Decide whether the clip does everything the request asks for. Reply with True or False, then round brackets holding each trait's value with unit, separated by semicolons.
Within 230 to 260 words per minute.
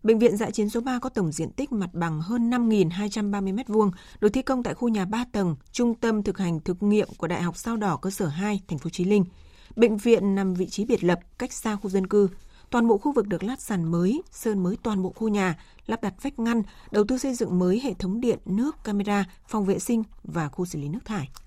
True (250 wpm)